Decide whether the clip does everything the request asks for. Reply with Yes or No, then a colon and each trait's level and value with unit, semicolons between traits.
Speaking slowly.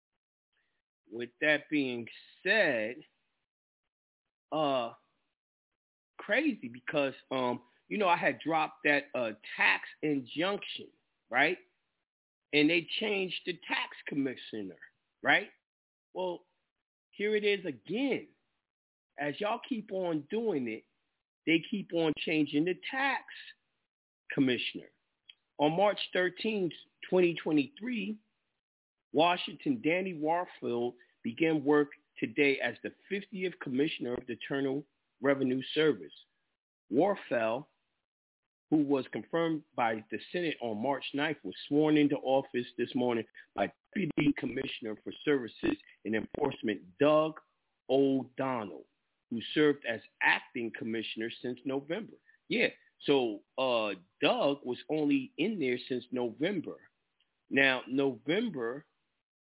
Yes: slow, 105 wpm